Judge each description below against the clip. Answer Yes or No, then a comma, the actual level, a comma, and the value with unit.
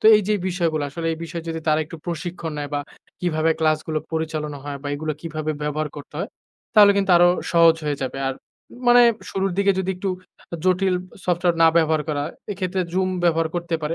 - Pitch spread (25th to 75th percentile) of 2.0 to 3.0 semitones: Yes, average, 2.7 semitones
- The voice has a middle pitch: Yes, medium, 165 Hz